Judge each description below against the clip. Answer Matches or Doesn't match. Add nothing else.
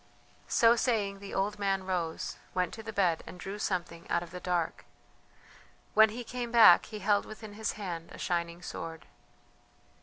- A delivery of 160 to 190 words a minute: Matches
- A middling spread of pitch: Matches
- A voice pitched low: Doesn't match